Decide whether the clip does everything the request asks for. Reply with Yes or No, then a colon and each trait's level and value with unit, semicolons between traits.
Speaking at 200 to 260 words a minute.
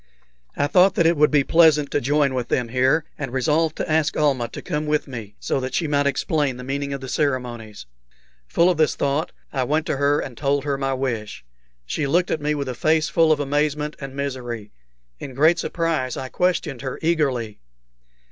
Yes: fast, 205 wpm